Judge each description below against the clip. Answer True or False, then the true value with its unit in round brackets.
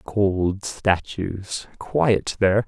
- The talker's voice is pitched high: False (95 Hz)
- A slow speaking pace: True (90 wpm)